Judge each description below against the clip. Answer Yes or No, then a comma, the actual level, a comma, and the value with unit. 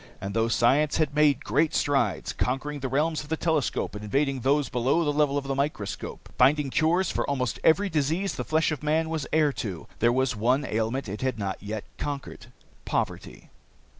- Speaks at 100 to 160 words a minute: No, average, 195 wpm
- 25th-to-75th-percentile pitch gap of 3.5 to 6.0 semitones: Yes, average, 3.9 semitones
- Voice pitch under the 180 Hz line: Yes, medium, 140 Hz